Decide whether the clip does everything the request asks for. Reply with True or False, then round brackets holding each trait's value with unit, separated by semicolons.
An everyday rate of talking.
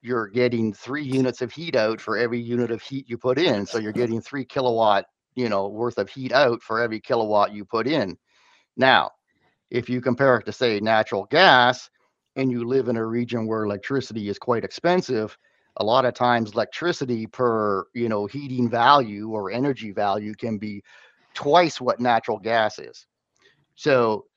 True (180 wpm)